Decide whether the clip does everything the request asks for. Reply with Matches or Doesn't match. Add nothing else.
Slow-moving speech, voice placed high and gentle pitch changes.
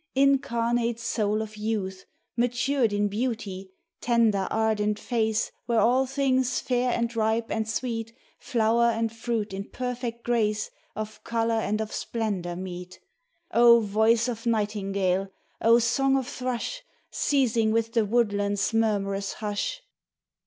Matches